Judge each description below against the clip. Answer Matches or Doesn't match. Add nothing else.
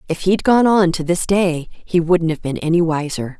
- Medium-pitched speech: Matches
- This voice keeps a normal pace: Doesn't match